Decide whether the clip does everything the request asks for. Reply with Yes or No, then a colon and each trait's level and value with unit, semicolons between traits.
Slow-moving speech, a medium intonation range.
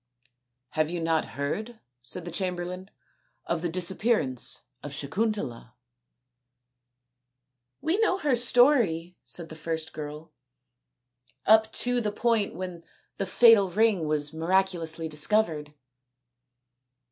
No: slow, 125 wpm; wide, 6.4 semitones